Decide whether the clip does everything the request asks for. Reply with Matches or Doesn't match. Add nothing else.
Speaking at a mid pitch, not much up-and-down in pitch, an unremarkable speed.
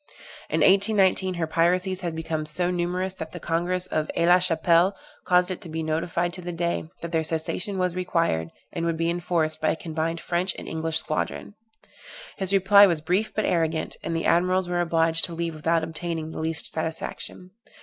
Matches